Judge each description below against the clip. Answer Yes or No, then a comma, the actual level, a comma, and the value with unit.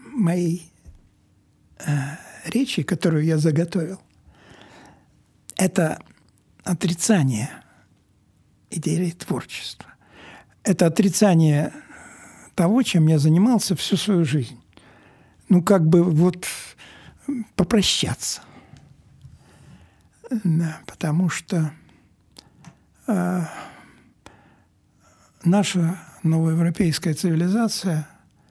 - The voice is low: No, medium, 170 Hz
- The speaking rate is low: Yes, slow, 65 wpm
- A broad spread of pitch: No, average, 3.5 semitones